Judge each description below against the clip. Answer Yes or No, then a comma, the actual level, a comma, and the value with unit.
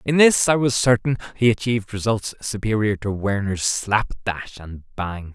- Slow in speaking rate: No, average, 170 wpm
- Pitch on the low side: Yes, low, 110 Hz